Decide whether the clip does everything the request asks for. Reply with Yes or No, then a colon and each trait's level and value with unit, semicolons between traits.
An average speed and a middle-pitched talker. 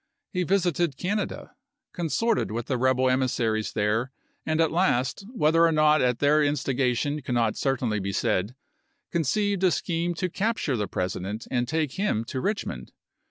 Yes: average, 160 wpm; medium, 145 Hz